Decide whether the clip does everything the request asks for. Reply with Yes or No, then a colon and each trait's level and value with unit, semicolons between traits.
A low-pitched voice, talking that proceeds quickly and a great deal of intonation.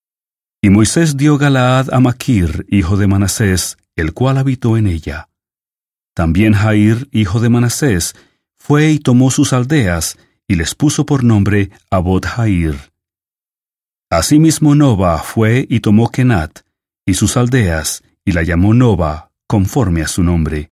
No: low, 105 Hz; slow, 135 wpm; wide, 6.2 semitones